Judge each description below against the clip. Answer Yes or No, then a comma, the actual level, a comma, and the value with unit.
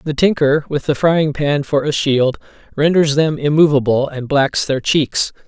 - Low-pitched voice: No, medium, 145 Hz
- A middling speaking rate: Yes, average, 175 wpm